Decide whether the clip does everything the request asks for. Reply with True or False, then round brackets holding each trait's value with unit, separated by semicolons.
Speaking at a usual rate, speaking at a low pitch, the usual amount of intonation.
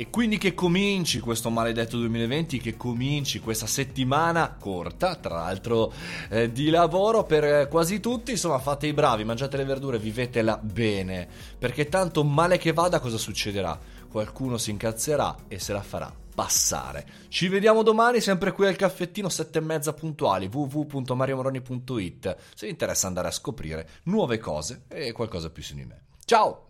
False (160 wpm; 130 Hz; 7.0 semitones)